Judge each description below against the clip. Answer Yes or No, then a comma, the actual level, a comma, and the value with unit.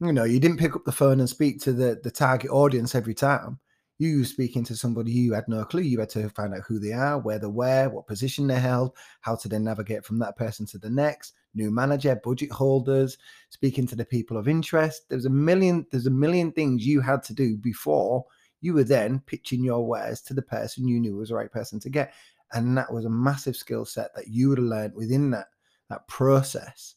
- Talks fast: Yes, fast, 235 wpm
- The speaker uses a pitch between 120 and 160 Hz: Yes, low, 130 Hz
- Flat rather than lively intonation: No, average, 3.2 semitones